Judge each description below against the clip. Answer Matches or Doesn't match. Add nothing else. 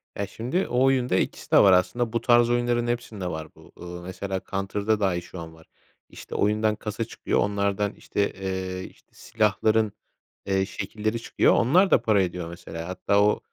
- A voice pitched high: Doesn't match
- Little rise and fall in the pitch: Doesn't match